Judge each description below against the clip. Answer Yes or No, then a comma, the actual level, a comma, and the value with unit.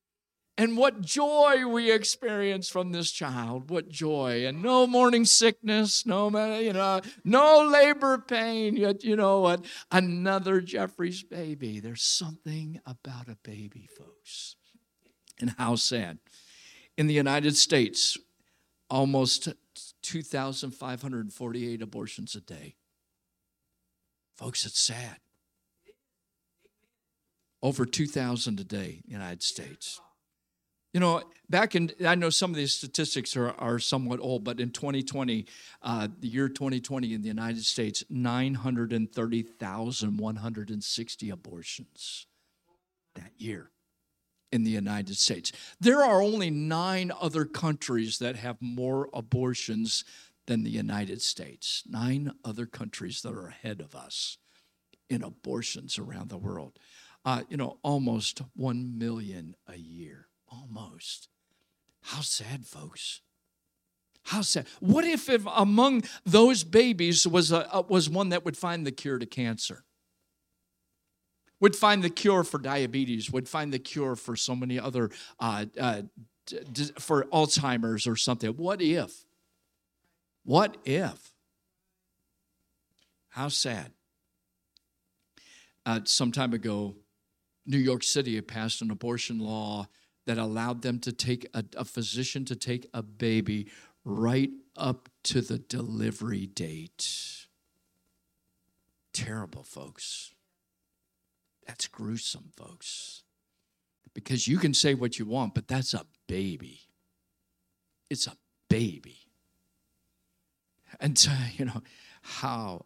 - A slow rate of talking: Yes, slow, 125 wpm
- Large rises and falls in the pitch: Yes, wide, 7.0 semitones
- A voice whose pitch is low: Yes, low, 125 Hz